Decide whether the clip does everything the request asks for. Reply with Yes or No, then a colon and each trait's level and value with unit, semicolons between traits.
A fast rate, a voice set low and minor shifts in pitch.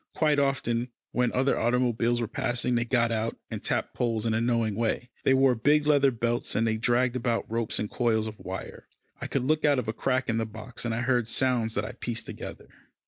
Yes: fast, 225 wpm; low, 120 Hz; narrow, 2.1 semitones